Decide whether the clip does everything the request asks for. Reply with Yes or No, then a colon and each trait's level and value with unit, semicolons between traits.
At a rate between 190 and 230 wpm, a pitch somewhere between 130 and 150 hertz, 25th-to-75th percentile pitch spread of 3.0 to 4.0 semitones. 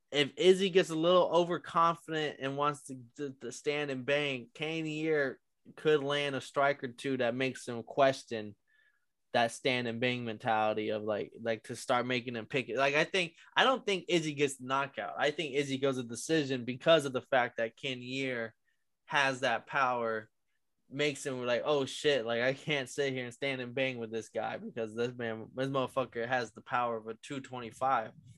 Yes: average, 200 wpm; low, 135 Hz; average, 3.6 semitones